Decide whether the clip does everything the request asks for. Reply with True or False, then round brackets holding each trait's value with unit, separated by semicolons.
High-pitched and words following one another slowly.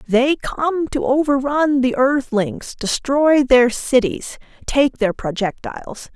True (265 Hz; 115 wpm)